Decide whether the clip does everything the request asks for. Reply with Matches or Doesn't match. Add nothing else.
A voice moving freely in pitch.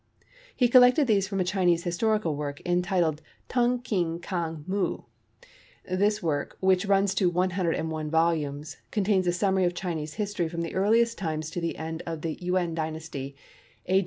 Doesn't match